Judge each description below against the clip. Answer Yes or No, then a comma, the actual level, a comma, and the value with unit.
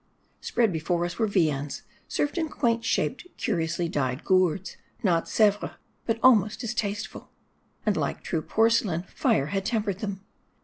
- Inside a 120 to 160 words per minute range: Yes, average, 145 wpm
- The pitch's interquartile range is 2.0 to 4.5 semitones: No, average, 5.0 semitones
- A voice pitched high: Yes, high, 195 Hz